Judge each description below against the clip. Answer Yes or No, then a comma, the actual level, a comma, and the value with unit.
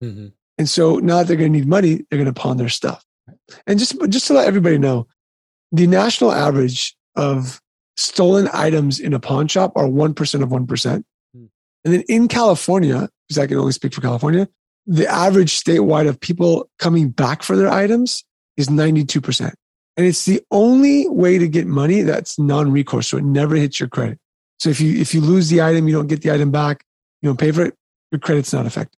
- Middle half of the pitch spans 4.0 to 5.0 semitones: Yes, average, 4.3 semitones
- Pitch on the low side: No, medium, 155 Hz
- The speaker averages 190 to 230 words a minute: Yes, fast, 205 wpm